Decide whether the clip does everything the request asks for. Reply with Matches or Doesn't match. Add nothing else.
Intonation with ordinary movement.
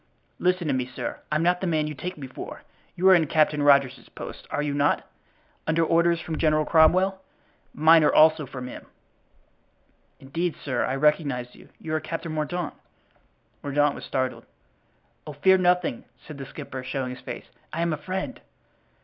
Matches